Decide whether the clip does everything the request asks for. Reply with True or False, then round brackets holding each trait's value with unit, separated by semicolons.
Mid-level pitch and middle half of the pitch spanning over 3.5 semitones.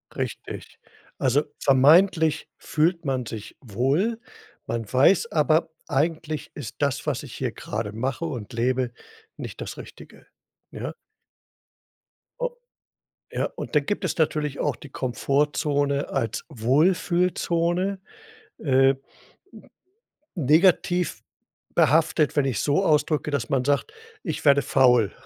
True (145 Hz; 4.1 semitones)